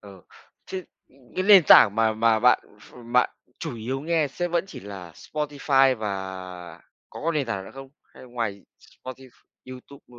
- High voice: No, low, 130 Hz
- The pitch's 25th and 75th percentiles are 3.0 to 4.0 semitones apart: No, average, 5.2 semitones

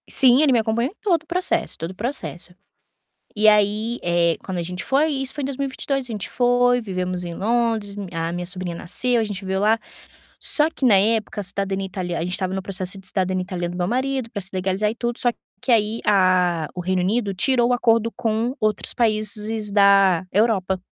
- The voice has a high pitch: Yes, high, 210 Hz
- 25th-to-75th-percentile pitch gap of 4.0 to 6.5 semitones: Yes, average, 4.4 semitones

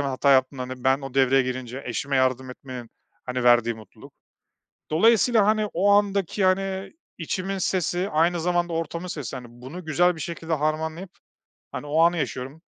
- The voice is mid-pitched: Yes, medium, 155 Hz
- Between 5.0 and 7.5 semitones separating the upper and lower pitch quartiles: Yes, wide, 5.5 semitones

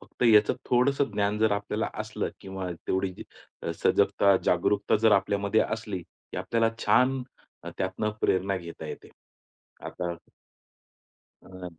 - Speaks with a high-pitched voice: No, low, 100 Hz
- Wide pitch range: No, average, 2.9 semitones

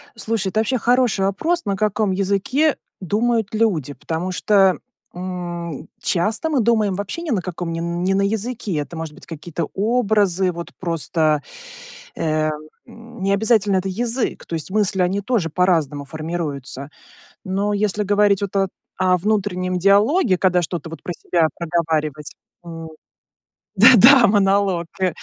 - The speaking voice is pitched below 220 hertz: Yes, high, 190 Hz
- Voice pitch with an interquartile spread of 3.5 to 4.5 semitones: Yes, average, 3.9 semitones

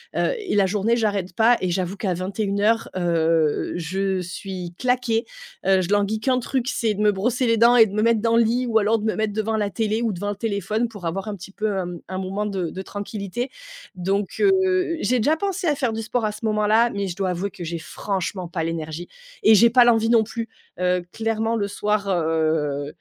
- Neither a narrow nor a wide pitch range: Yes, average, 3.5 semitones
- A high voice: Yes, high, 210 Hz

